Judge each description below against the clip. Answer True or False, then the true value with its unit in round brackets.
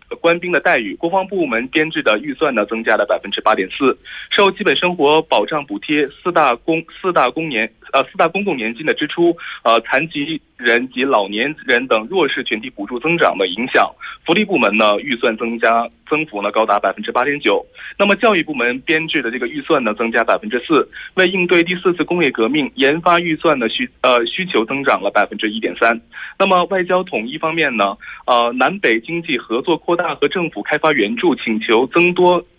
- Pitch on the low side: False (155 Hz)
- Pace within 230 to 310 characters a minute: True (305 characters per minute)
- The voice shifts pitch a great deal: True (7.3 semitones)